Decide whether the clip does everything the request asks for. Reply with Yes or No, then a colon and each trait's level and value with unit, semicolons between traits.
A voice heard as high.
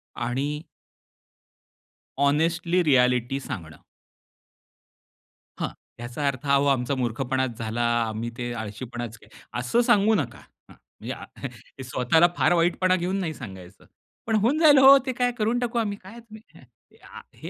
No: medium, 140 Hz